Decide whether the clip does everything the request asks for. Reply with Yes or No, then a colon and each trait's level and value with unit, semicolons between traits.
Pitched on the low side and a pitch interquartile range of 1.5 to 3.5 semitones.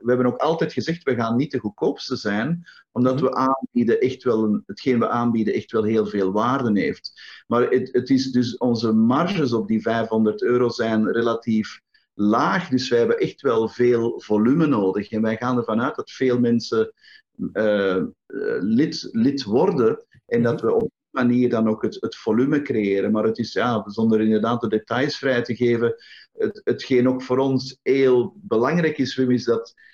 Yes: low, 120 Hz; average, 3.0 semitones